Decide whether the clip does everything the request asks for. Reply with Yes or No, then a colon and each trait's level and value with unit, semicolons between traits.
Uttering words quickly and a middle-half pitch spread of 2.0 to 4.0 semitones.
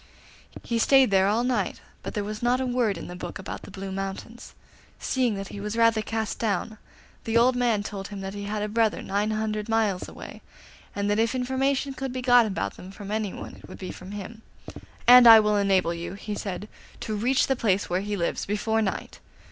Yes: fast, 220 wpm; average, 2.8 semitones